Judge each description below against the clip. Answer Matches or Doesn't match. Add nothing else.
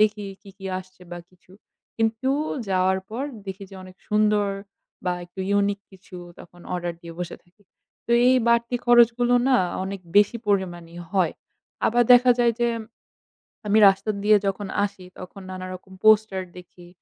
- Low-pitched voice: Doesn't match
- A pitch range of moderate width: Matches